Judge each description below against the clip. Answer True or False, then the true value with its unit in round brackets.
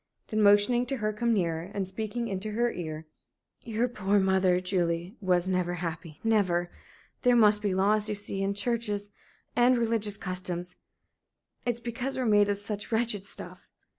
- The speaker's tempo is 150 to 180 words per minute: True (165 wpm)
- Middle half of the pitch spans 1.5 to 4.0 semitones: True (3.5 semitones)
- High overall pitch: True (205 Hz)